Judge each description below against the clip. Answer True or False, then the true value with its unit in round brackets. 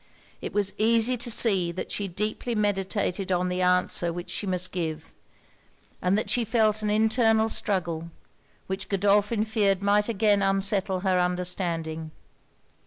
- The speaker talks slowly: False (145 wpm)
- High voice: True (195 Hz)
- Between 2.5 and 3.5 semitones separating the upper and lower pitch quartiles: True (2.9 semitones)